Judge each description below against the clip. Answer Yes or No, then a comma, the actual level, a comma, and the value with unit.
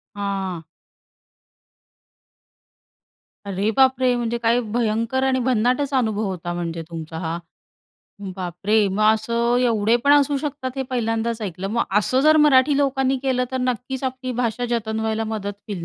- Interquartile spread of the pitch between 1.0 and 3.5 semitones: No, average, 4.2 semitones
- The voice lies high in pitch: Yes, high, 230 Hz